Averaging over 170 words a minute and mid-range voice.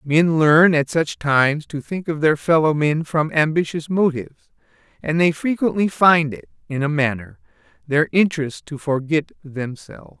No: average, 160 wpm; medium, 155 Hz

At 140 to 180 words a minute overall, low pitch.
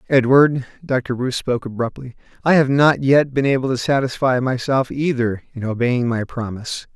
Yes: average, 165 wpm; low, 130 Hz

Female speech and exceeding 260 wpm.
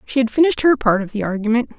Yes: female; fast, 270 wpm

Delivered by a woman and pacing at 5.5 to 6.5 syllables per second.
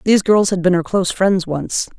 Yes: female; 5.6 syllables/s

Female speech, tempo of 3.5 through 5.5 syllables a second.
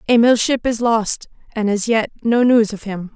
Yes: female; 4.6 syllables/s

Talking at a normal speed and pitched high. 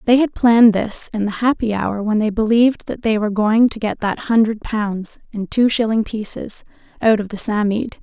No: fast, 210 wpm; high, 220 Hz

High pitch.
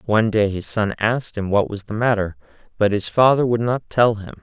No: low, 110 Hz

